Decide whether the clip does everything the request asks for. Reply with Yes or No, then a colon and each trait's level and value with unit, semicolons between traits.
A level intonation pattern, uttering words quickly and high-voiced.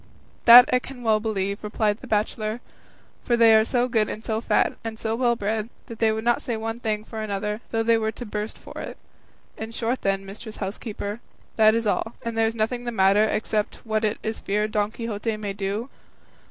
Yes: narrow, 1.5 semitones; fast, 215 wpm; high, 220 Hz